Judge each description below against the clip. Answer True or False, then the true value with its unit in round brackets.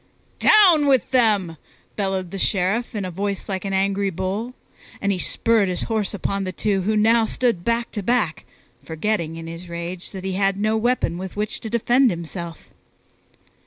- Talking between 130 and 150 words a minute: False (180 wpm)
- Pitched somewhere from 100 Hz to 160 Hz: False (200 Hz)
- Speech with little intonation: False (3.5 semitones)